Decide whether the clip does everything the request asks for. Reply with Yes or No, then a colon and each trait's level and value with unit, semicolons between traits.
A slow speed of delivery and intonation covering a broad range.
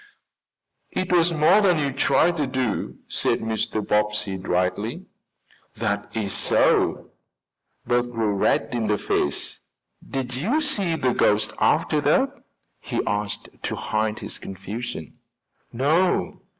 Yes: slow, 125 wpm; wide, 6.7 semitones